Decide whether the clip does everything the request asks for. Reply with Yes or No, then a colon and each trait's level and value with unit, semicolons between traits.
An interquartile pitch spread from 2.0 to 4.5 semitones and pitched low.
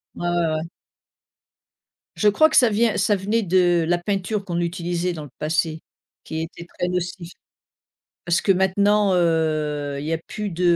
No: average, 3.2 semitones; medium, 175 Hz